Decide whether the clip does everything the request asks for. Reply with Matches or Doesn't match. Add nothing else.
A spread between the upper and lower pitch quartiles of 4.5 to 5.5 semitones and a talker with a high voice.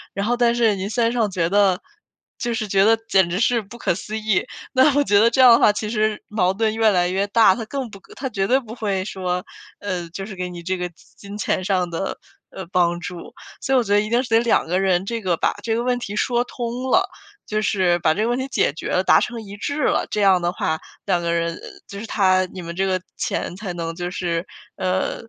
Doesn't match